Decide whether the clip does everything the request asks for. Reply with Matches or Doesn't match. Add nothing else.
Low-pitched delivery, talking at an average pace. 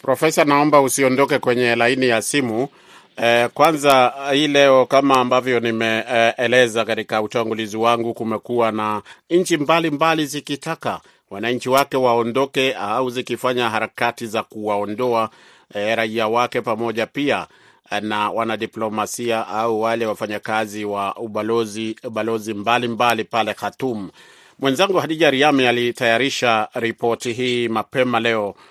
Matches